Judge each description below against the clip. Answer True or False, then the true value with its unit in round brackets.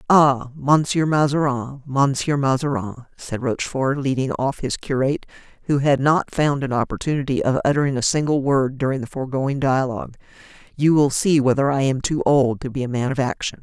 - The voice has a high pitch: False (135 Hz)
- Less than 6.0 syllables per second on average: True (5.4 syllables/s)